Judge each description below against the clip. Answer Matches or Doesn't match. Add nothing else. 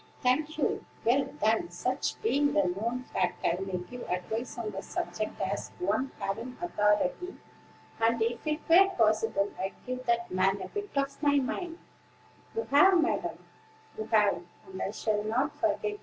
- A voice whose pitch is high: Matches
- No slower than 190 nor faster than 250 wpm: Doesn't match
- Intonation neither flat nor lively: Doesn't match